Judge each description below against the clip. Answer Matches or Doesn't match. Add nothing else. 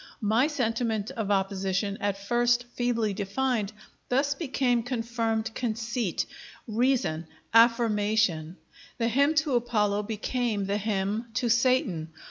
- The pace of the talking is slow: Matches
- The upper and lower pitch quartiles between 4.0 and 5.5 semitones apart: Doesn't match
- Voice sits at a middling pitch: Doesn't match